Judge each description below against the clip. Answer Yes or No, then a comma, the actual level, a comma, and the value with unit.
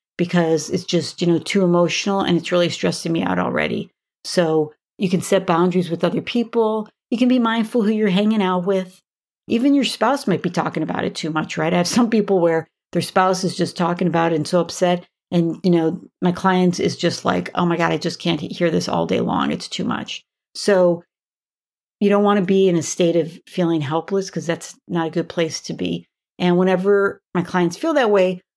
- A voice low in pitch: No, medium, 180 Hz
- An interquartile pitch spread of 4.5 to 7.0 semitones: No, narrow, 2.6 semitones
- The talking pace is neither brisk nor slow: No, fast, 225 wpm